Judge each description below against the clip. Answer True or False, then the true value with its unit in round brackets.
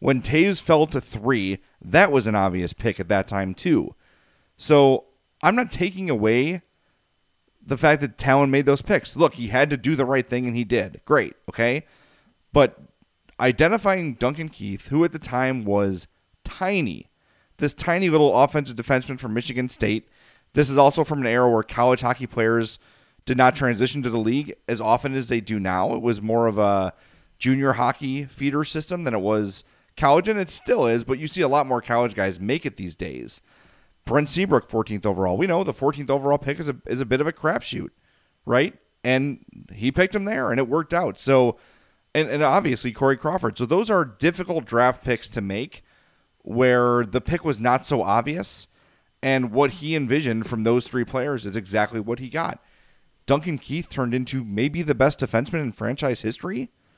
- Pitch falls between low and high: False (130 Hz)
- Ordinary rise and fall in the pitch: True (4.1 semitones)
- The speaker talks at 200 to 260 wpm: False (190 wpm)